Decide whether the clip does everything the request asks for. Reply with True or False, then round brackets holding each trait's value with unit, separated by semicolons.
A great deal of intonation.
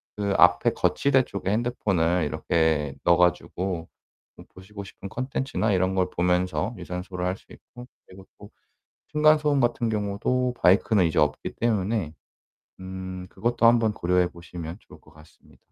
False (4.6 semitones)